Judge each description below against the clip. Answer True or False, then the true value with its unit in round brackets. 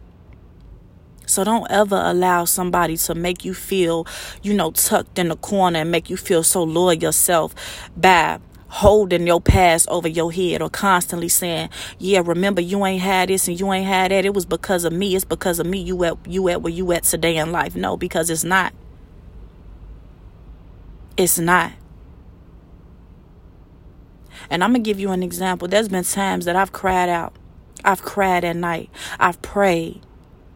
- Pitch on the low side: False (175 Hz)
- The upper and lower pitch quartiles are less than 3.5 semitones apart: True (2.5 semitones)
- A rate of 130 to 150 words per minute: False (175 wpm)